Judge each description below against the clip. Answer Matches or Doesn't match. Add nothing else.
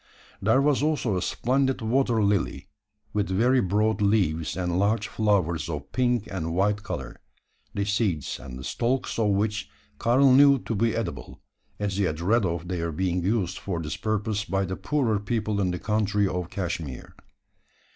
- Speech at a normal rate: Matches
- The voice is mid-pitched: Doesn't match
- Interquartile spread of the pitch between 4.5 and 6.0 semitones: Doesn't match